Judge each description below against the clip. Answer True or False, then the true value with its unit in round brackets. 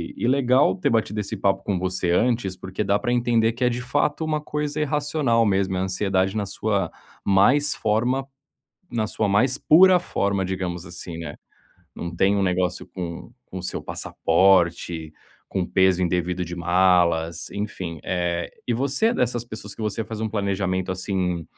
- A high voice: False (100 Hz)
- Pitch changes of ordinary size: True (4.6 semitones)